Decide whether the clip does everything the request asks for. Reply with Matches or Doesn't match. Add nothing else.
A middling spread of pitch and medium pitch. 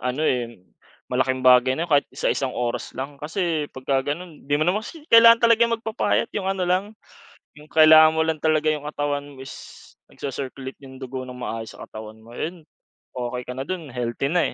Matches